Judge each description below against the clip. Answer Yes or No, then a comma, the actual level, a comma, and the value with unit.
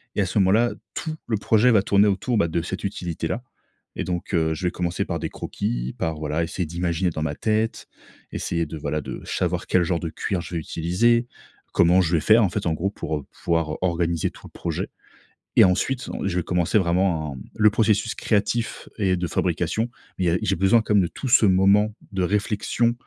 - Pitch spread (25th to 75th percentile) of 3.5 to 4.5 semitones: Yes, average, 4.0 semitones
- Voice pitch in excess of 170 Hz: No, very low, 90 Hz